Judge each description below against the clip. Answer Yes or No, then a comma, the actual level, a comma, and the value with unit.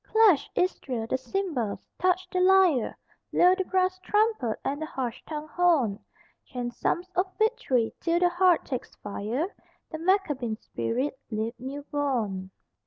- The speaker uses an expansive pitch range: Yes, wide, 7.1 semitones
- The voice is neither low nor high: No, very high, 305 Hz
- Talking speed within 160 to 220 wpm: No, average, 145 wpm